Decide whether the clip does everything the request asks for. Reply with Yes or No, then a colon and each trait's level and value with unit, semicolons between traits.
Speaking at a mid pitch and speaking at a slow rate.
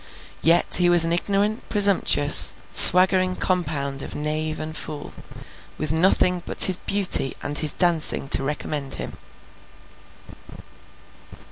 Yes: medium, 165 Hz; slow, 120 wpm